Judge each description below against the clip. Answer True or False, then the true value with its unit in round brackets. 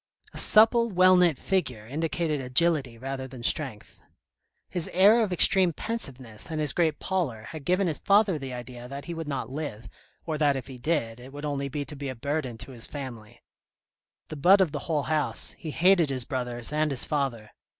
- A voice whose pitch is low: False (145 Hz)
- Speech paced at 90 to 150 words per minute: False (200 wpm)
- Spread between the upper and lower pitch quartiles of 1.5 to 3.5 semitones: False (4.8 semitones)